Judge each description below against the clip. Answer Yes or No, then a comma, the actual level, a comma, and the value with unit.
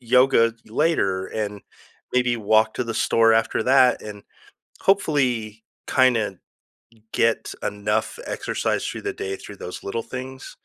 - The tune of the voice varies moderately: Yes, average, 3.4 semitones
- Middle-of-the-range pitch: No, low, 115 Hz